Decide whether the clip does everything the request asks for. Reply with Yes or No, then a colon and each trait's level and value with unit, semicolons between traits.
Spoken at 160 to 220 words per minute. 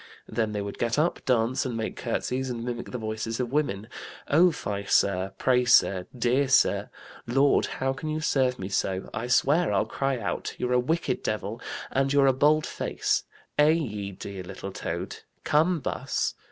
Yes: average, 180 wpm